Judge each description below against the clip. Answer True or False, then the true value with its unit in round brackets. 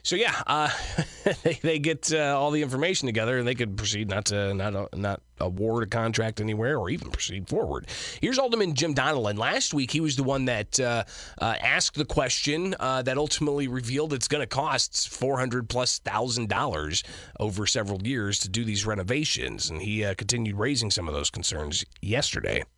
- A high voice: False (120 Hz)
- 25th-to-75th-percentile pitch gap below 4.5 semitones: False (5.4 semitones)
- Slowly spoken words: False (195 wpm)